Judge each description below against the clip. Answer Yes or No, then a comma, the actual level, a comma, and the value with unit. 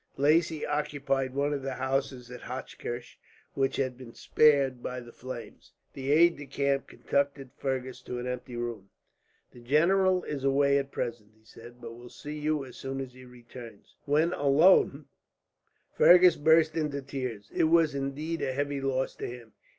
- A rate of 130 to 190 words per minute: Yes, average, 170 wpm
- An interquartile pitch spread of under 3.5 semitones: Yes, average, 2.8 semitones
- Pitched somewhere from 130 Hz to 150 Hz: Yes, low, 135 Hz